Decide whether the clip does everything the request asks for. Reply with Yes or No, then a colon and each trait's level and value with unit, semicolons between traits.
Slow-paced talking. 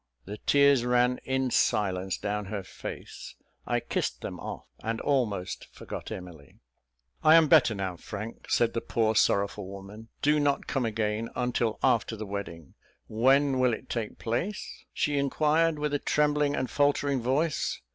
No: average, 160 wpm